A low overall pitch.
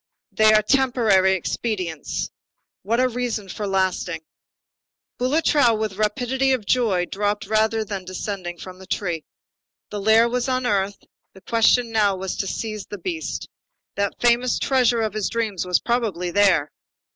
No: high, 215 Hz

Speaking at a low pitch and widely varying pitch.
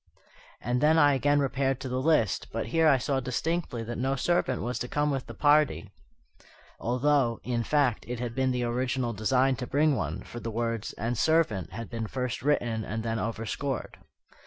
No: low, 125 Hz; average, 3.5 semitones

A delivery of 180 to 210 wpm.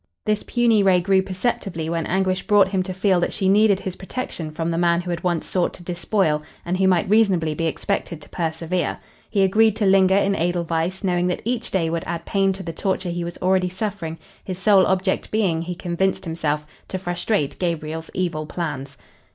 Yes: average, 200 wpm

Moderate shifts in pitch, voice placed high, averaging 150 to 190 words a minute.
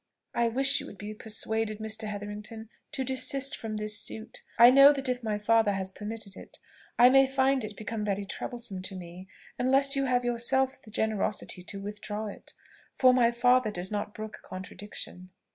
Yes: average, 3.4 semitones; high, 220 Hz; average, 180 wpm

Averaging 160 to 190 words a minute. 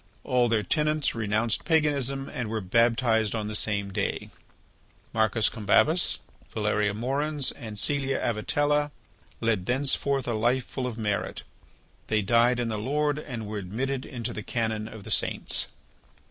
No: average, 145 wpm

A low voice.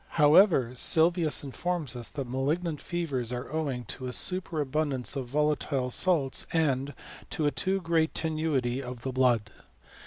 No: medium, 145 Hz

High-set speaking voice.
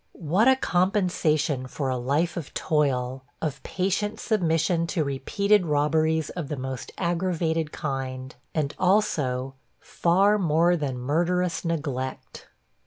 No: medium, 160 Hz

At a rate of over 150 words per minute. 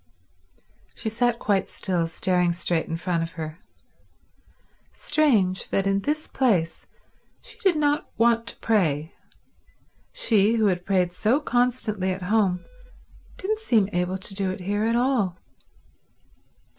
No: slow, 135 wpm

